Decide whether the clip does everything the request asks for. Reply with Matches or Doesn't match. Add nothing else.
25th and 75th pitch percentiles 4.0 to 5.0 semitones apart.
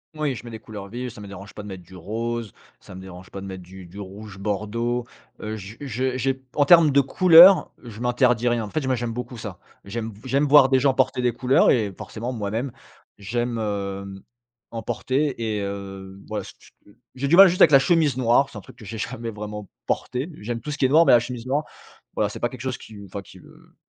Matches